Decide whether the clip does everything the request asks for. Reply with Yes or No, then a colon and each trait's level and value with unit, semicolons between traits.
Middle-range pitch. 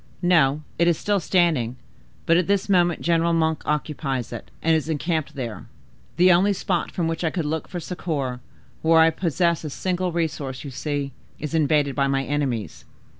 Yes: medium, 160 Hz